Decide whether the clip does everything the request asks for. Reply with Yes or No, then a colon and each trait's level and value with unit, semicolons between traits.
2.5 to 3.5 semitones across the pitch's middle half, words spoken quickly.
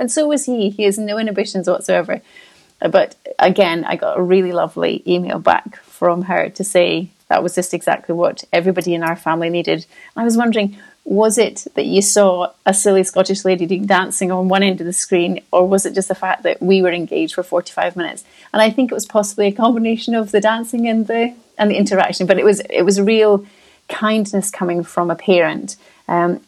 Yes: average, 3.0 semitones; fast, 210 wpm